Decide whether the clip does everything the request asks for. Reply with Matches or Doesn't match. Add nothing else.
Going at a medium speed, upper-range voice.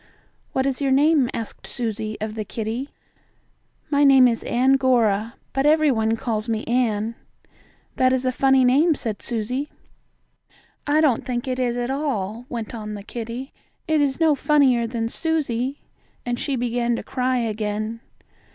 Matches